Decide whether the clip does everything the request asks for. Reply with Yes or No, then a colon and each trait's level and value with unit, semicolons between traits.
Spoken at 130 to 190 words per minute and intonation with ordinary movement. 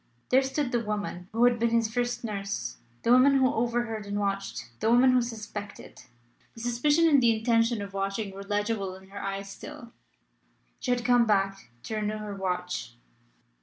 Yes: average, 180 wpm; average, 3.5 semitones